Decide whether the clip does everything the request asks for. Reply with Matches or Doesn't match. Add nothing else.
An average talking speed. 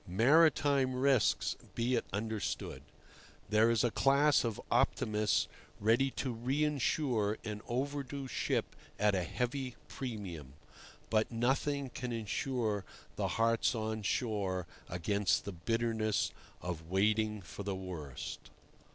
Doesn't match